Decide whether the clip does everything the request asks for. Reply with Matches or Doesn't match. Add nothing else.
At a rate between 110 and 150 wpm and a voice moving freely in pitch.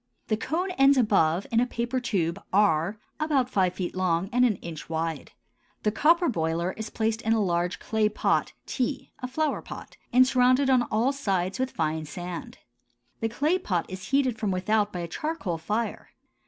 Doesn't match